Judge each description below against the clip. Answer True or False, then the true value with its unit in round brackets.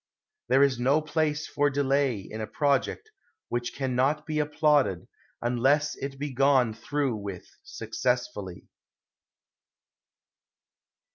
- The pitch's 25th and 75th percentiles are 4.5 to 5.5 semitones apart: False (3.3 semitones)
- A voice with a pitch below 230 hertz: True (135 Hz)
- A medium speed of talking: False (115 wpm)